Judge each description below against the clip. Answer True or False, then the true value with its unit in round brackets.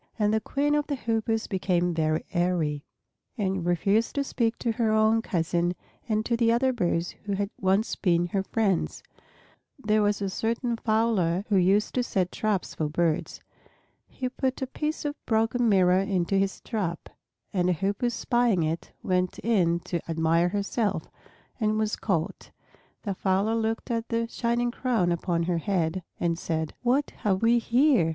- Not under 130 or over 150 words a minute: False (170 wpm)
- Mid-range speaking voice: False (205 Hz)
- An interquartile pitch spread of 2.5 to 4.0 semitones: False (4.6 semitones)